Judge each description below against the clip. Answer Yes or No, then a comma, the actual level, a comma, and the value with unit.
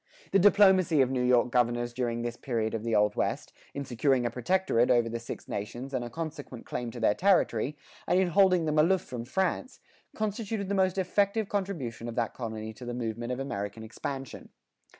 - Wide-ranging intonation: Yes, wide, 7.8 semitones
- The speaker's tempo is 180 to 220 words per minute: Yes, average, 195 wpm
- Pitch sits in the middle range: No, low, 125 Hz